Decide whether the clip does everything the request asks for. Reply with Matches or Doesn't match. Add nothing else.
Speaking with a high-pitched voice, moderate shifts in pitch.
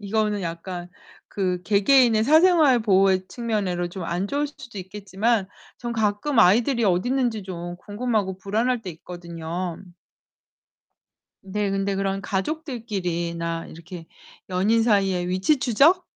Matches